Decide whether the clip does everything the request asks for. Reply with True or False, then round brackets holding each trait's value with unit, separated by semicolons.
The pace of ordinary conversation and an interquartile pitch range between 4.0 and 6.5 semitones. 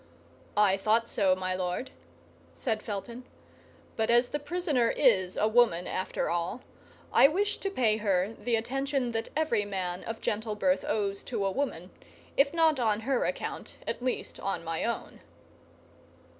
True (155 wpm; 4.8 semitones)